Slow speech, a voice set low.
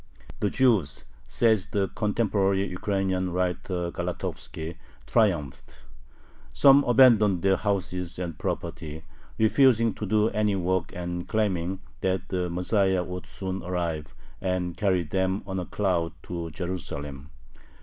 Yes: slow, 120 wpm; very low, 95 Hz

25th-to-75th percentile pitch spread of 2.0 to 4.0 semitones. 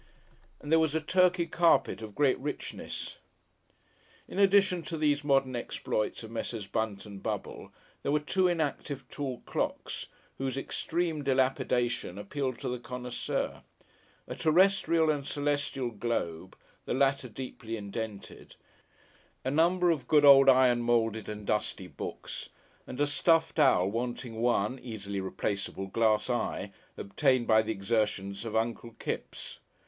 No: average, 4.9 semitones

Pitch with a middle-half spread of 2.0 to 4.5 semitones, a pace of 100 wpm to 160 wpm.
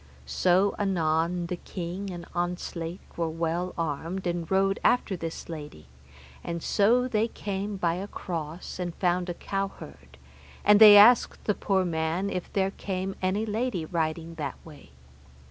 Yes: average, 3.0 semitones; average, 150 wpm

